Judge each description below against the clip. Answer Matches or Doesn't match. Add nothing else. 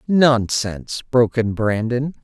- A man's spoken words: Matches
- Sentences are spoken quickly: Doesn't match